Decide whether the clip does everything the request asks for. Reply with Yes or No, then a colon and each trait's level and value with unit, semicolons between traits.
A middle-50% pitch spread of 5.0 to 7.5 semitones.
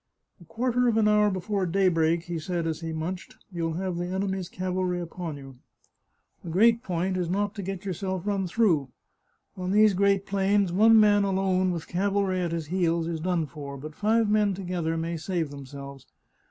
No: average, 3.2 semitones